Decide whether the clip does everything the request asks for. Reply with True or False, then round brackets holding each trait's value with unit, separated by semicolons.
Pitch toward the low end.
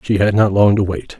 True (100 Hz)